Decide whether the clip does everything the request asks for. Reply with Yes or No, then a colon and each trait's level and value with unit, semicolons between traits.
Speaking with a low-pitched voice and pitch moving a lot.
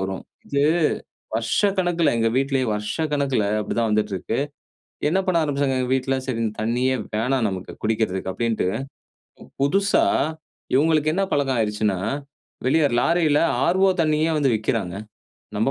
Yes: low, 130 Hz; wide, 5.8 semitones